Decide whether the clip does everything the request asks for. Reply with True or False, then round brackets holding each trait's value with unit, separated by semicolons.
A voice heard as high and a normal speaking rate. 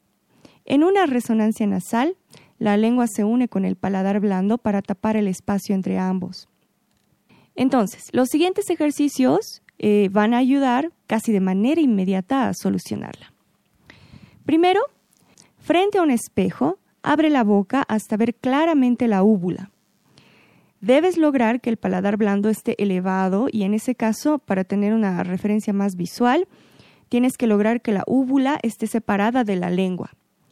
True (220 Hz; 145 wpm)